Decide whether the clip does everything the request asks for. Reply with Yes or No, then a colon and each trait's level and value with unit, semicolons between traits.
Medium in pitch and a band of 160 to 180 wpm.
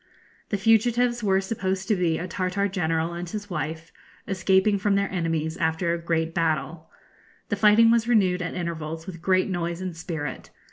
Yes: medium, 180 Hz; average, 175 wpm